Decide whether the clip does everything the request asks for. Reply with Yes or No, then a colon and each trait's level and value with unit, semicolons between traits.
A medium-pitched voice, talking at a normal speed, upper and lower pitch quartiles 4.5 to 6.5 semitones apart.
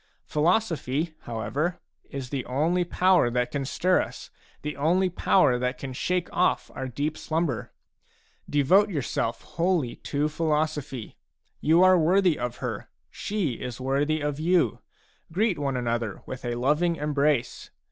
Yes: medium, 150 Hz; average, 145 wpm; average, 5.1 semitones